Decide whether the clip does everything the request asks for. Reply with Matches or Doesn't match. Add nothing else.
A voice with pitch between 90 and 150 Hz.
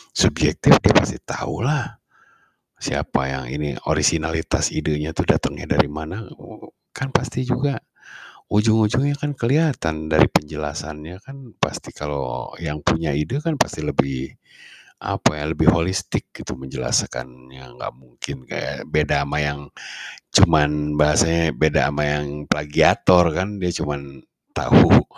Doesn't match